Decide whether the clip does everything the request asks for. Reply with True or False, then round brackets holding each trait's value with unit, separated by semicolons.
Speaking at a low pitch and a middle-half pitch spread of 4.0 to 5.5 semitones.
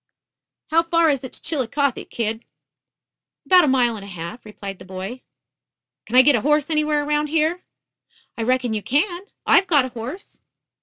False (265 Hz; 5.2 semitones)